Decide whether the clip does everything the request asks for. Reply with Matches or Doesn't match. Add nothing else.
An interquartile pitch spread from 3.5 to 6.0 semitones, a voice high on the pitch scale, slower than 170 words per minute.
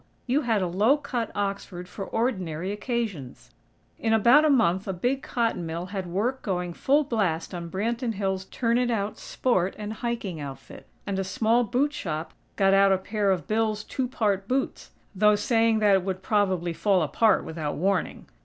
Doesn't match